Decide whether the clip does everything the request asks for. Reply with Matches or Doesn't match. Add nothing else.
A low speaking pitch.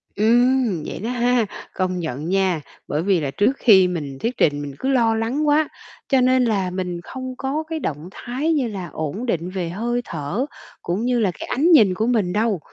Doesn't match